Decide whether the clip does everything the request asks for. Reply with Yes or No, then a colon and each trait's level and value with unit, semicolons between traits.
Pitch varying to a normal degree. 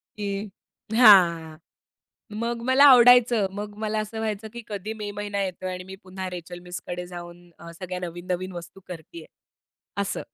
Yes: average, 3.3 semitones